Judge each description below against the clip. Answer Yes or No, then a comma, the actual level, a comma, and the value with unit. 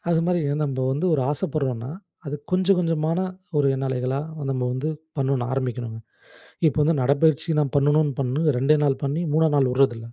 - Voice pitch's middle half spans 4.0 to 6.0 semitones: No, average, 3.2 semitones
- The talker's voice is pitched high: No, medium, 140 Hz